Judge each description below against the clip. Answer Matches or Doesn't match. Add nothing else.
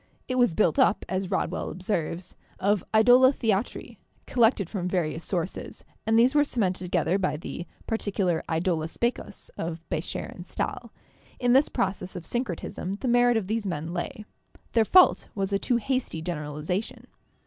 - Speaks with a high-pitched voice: Matches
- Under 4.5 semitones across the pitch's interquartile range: Doesn't match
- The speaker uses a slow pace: Doesn't match